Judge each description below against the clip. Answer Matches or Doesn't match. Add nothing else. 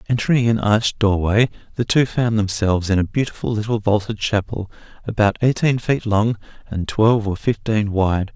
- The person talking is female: Doesn't match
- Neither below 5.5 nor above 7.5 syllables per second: Doesn't match